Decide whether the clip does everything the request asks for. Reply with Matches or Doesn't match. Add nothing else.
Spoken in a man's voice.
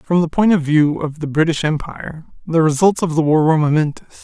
Matches